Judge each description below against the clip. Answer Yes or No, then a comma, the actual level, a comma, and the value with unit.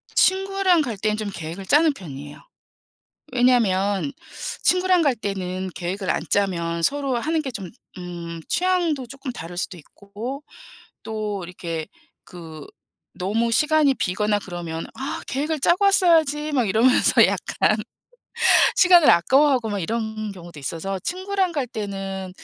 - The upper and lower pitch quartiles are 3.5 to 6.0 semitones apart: No, wide, 8.1 semitones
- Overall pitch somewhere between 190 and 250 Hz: Yes, high, 220 Hz